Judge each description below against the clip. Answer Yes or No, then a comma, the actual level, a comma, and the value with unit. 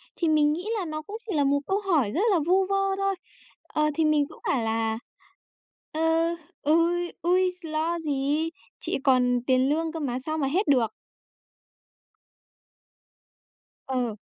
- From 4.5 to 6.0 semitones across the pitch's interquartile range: No, average, 4.0 semitones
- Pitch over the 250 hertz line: Yes, very high, 310 Hz